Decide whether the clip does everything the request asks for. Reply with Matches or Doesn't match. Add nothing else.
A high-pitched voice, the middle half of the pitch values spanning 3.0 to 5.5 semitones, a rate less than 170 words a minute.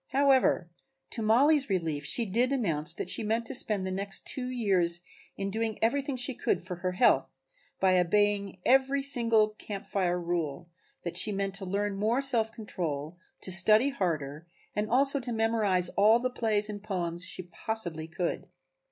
Doesn't match